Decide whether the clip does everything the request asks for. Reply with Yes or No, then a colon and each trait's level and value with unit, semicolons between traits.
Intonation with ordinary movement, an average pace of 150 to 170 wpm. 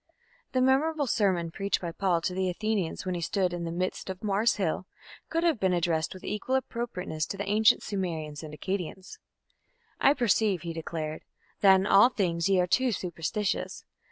No: average, 3.9 semitones; average, 185 wpm